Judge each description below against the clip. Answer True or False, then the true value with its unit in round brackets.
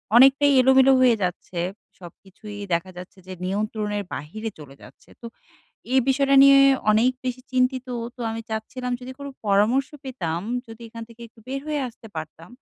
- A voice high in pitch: True (230 Hz)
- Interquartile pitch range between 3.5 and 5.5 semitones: True (4.8 semitones)